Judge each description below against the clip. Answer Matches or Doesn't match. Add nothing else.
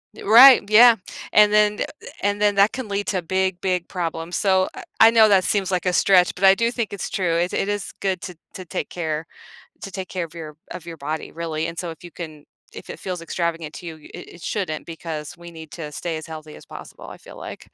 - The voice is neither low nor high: Matches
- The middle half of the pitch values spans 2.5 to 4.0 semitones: Matches